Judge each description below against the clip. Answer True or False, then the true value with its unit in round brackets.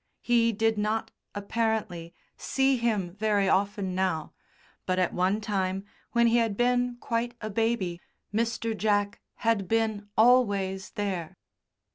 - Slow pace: True (130 wpm)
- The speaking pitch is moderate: False (210 Hz)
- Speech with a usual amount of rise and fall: True (3.2 semitones)